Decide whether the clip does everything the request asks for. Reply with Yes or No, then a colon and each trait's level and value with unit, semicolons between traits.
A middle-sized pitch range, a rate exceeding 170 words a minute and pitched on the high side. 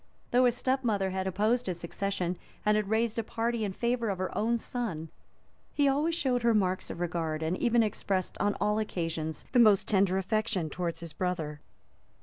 Yes: average, 4.6 semitones; average, 190 wpm; high, 205 Hz